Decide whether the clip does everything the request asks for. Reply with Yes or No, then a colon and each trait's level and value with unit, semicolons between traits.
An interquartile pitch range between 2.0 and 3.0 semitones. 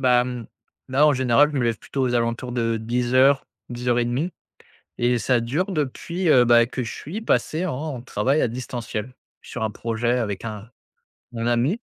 Yes: narrow, 2.6 semitones